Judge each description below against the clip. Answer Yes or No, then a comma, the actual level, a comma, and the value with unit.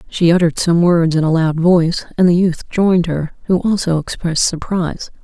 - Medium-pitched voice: Yes, medium, 170 Hz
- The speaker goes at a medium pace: Yes, average, 195 wpm